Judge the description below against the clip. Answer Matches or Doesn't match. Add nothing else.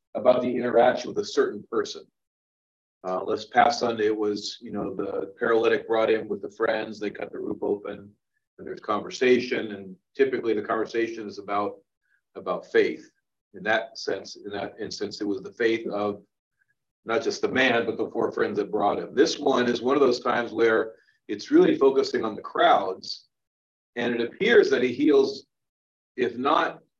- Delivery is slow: Doesn't match